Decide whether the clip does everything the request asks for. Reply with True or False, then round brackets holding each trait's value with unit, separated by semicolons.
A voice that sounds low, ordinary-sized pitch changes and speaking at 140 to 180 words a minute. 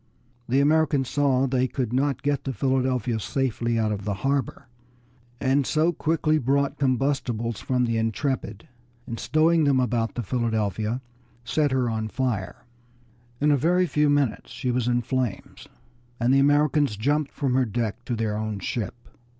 True (130 Hz; 3.6 semitones; 165 wpm)